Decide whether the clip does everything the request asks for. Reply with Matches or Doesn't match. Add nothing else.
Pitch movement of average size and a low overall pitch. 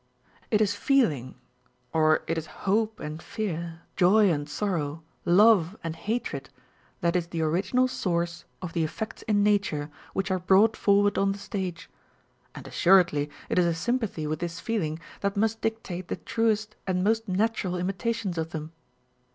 Doesn't match